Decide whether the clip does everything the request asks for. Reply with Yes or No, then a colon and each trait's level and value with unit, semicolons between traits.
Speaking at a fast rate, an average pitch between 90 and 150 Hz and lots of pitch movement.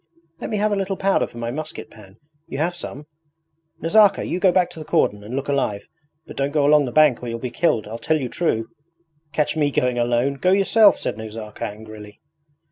Yes: fast, 215 wpm; medium, 140 Hz; wide, 6.8 semitones